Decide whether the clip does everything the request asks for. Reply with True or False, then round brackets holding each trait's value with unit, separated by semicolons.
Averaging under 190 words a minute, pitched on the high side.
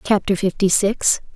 True (135 wpm; 200 Hz)